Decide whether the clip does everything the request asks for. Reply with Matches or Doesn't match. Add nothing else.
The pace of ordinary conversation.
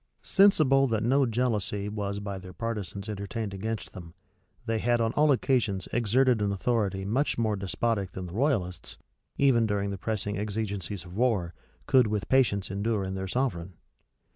Matches